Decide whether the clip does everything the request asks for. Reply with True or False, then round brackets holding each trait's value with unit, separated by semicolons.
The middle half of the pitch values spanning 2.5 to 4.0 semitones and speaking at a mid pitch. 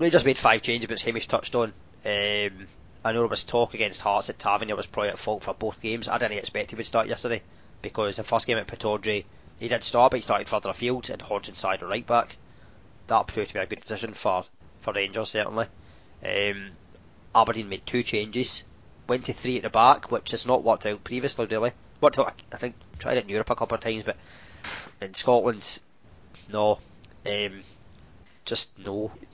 False (3.0 semitones; 110 Hz)